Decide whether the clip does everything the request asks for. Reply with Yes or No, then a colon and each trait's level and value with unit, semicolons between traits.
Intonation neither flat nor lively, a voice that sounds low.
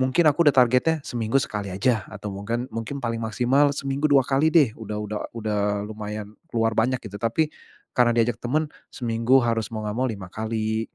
Yes: average, 3.5 semitones; low, 115 Hz